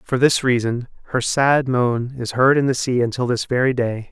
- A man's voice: Yes, male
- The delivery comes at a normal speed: No, fast, 220 wpm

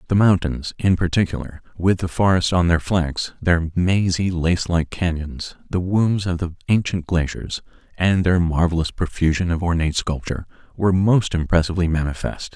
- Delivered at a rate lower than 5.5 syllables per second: Yes, 5.2 syllables/s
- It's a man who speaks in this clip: Yes, male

